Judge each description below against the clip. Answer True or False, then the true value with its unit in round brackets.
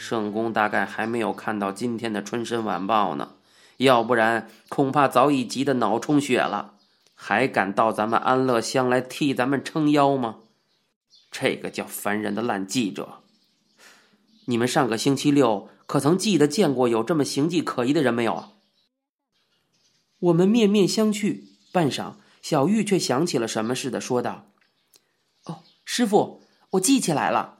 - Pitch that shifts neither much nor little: False (7.0 semitones)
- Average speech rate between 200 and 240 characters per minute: True (235 characters per minute)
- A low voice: True (125 Hz)